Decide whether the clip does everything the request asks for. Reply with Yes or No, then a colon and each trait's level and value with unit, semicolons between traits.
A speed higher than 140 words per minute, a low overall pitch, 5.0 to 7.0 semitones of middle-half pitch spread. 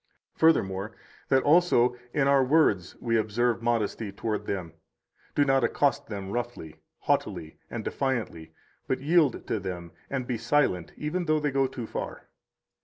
Yes: average, 155 wpm; low, 120 Hz; wide, 5.6 semitones